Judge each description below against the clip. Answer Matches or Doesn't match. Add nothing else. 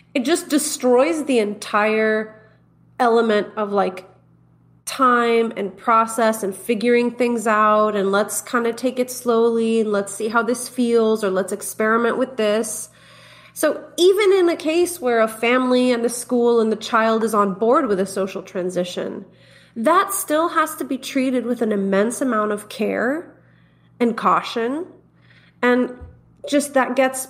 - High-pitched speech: Matches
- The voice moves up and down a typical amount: Matches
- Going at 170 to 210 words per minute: Doesn't match